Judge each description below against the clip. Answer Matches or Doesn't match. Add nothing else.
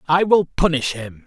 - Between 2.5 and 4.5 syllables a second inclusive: Doesn't match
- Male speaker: Matches